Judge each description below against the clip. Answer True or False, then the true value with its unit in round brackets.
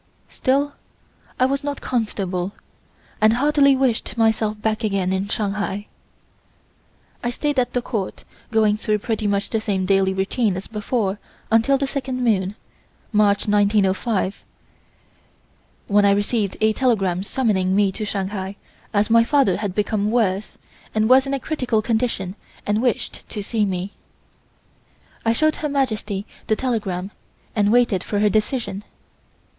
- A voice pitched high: True (215 Hz)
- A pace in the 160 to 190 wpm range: False (145 wpm)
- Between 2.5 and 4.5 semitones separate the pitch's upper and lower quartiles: True (3.4 semitones)